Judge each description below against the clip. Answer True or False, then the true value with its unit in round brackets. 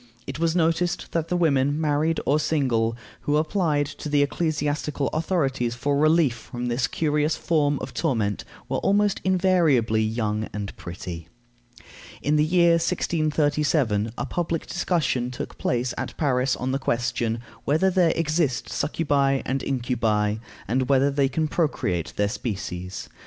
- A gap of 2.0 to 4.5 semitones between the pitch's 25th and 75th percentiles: False (4.9 semitones)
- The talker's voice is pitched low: False (145 Hz)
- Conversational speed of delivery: True (145 wpm)